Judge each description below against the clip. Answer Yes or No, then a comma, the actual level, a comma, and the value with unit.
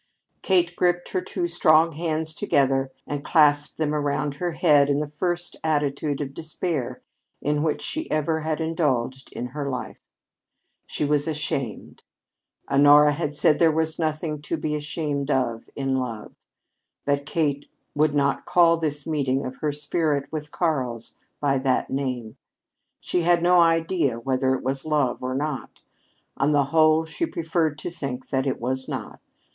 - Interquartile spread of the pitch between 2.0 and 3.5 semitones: Yes, average, 2.7 semitones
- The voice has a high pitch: No, medium, 150 Hz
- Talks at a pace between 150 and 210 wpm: Yes, average, 160 wpm